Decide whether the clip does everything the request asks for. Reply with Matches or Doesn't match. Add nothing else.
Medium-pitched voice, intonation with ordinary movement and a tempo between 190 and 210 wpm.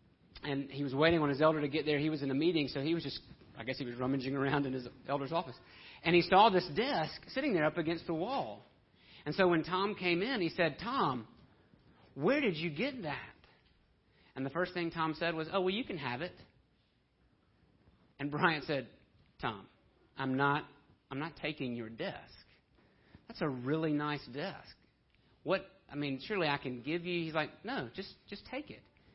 Matches